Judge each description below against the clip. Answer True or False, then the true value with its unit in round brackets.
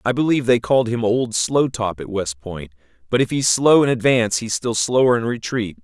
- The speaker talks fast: True (225 wpm)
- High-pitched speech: False (115 Hz)